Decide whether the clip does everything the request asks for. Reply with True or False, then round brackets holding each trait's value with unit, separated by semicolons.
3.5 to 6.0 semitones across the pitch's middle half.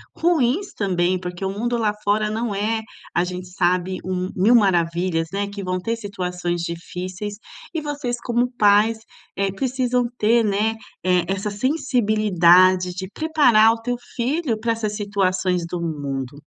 True (4.0 semitones)